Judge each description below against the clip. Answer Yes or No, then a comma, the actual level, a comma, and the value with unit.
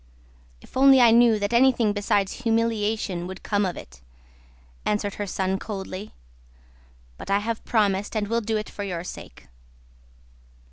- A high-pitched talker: Yes, high, 210 Hz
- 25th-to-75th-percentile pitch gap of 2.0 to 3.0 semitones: Yes, average, 2.7 semitones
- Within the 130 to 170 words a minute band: Yes, average, 150 wpm